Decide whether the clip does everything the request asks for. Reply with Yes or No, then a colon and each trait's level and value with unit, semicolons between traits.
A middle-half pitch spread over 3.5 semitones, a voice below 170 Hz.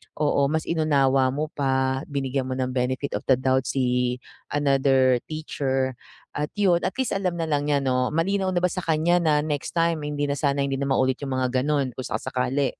No: average, 2.9 semitones; medium, 140 Hz